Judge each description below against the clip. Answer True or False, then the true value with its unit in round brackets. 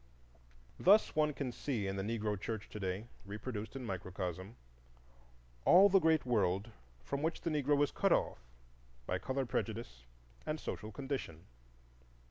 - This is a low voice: True (115 Hz)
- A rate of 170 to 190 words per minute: False (145 wpm)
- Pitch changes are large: True (6.6 semitones)